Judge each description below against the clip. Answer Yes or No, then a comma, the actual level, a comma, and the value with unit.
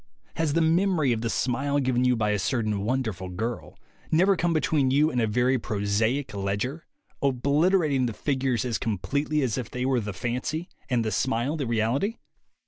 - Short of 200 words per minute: Yes, average, 185 wpm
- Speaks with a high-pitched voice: No, low, 125 Hz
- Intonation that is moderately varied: Yes, average, 4.4 semitones